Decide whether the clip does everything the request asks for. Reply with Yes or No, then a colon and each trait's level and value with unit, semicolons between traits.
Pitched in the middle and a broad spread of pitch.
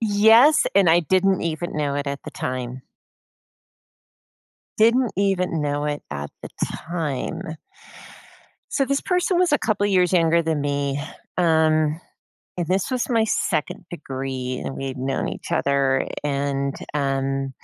Yes: medium, 160 Hz; wide, 5.8 semitones